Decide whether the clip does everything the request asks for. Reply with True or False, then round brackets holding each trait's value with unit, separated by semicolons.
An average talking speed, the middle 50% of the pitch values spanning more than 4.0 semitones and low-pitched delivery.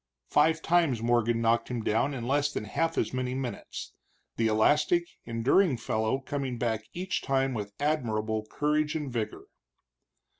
True (150 wpm; 4.5 semitones; 130 Hz)